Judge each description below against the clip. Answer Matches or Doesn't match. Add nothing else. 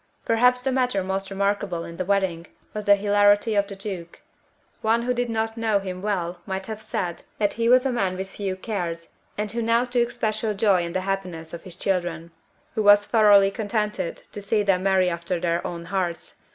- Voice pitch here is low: Doesn't match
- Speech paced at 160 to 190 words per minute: Doesn't match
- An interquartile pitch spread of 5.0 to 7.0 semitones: Doesn't match